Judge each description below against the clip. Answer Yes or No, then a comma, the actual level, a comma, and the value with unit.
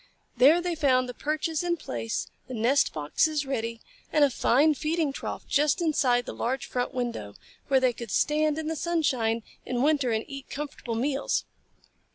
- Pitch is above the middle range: Yes, very high, 275 Hz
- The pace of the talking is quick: No, average, 175 wpm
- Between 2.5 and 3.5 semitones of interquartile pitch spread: No, average, 4.0 semitones